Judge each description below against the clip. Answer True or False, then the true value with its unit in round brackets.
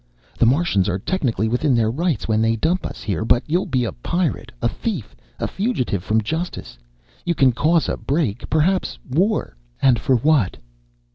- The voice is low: True (130 Hz)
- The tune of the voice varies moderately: False (7.2 semitones)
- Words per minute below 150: False (180 wpm)